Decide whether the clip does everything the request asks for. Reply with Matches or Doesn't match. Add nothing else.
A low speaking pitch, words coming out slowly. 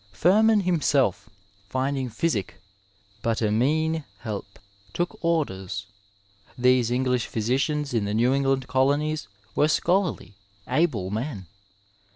Matches